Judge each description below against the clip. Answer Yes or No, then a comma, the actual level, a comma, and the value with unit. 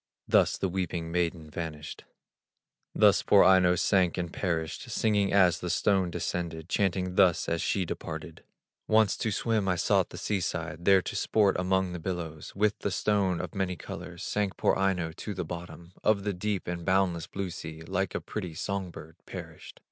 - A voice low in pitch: Yes, very low, 90 Hz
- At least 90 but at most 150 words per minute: No, average, 180 wpm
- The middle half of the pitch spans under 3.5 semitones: Yes, narrow, 2.4 semitones